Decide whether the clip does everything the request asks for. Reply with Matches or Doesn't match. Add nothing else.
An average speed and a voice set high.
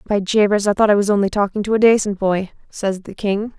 Doesn't match